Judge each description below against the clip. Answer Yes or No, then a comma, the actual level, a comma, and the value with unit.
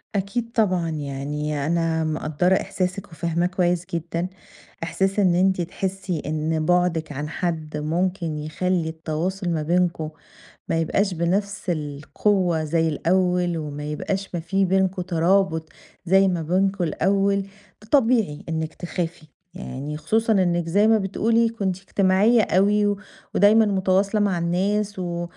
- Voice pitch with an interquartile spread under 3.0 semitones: No, average, 3.3 semitones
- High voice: No, medium, 180 Hz